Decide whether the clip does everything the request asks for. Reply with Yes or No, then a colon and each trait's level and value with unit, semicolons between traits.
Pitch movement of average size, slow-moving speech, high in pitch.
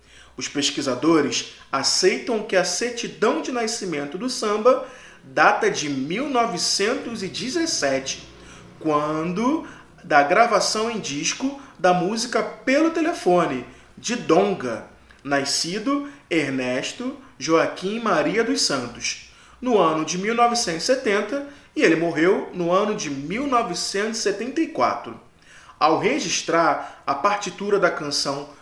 No: wide, 7.5 semitones; slow, 100 wpm; high, 205 Hz